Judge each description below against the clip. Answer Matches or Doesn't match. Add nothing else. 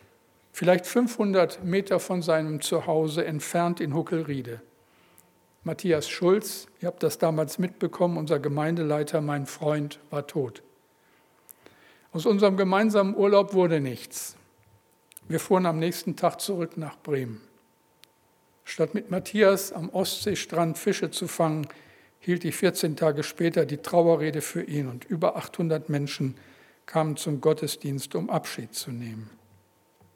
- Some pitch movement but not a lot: Matches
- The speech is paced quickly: Doesn't match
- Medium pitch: Matches